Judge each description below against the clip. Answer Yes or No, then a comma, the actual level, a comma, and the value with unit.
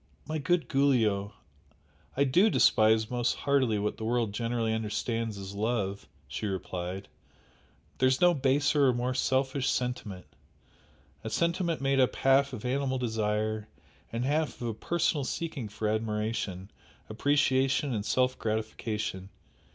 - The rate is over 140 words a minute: No, slow, 135 wpm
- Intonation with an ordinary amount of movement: Yes, average, 4.1 semitones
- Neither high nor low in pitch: No, low, 120 Hz